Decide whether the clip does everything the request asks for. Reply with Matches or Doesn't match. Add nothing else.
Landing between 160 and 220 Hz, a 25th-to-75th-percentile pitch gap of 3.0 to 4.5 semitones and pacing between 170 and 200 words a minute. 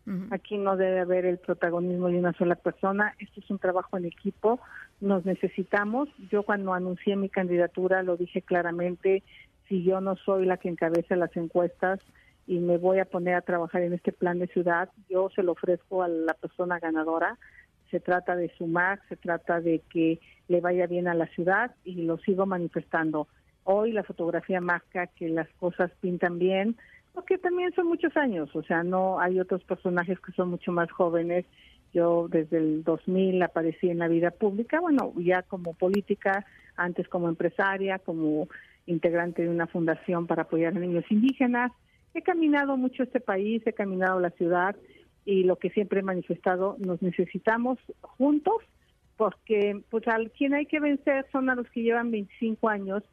Doesn't match